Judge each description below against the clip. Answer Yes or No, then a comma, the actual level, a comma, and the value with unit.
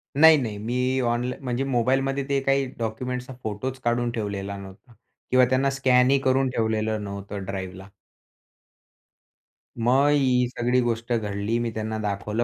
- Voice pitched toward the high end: No, low, 120 Hz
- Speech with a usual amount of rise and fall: Yes, average, 3.3 semitones